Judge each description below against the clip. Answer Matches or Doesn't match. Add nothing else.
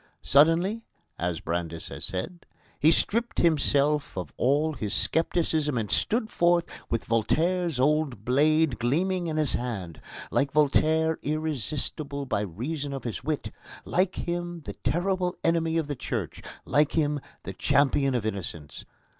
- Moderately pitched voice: Matches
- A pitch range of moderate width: Matches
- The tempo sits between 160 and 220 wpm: Doesn't match